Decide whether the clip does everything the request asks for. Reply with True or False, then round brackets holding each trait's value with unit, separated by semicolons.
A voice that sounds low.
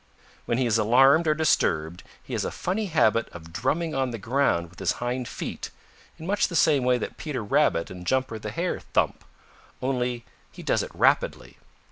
True (125 Hz)